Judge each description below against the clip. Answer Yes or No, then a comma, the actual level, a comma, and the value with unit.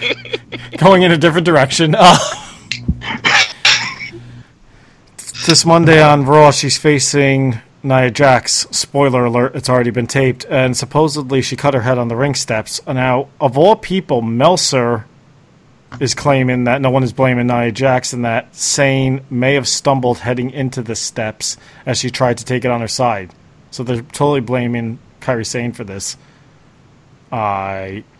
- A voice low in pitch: Yes, low, 130 Hz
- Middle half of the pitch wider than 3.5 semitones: No, average, 2.7 semitones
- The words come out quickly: No, average, 155 wpm